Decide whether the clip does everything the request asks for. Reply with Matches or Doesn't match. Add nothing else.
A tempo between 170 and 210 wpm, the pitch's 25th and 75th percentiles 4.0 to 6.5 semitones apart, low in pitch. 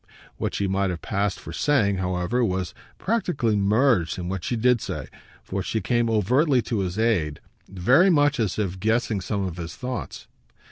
Matches